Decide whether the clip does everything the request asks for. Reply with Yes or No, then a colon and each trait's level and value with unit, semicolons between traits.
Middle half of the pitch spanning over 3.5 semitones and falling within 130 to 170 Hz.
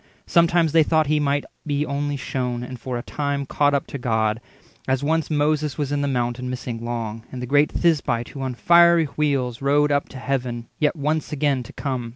No: average, 3.2 semitones; medium, 140 Hz